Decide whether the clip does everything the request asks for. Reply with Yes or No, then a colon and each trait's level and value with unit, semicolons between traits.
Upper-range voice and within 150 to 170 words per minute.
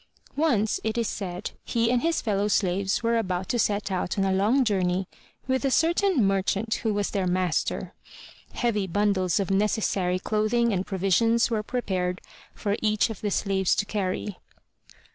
Yes: high, 205 Hz; average, 165 wpm